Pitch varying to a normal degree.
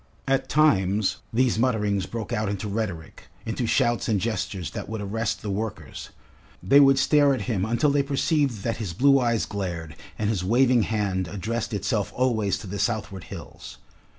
Yes: average, 3.9 semitones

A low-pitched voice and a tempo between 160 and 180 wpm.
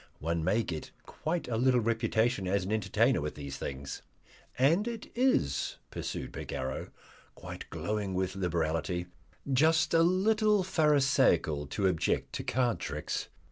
No: low, 110 Hz; average, 140 wpm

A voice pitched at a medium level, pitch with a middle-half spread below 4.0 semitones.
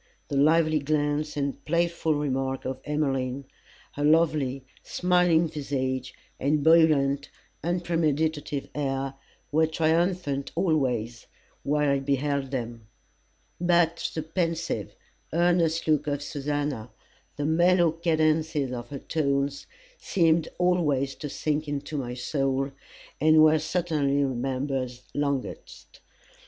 Yes: medium, 150 Hz; average, 2.7 semitones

